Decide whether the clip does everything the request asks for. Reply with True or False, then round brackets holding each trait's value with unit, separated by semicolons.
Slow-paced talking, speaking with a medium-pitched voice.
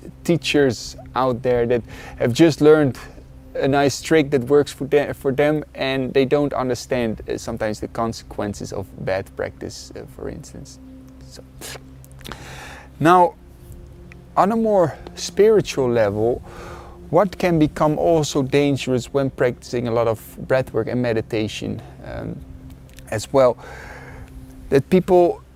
False (130 wpm; 125 Hz)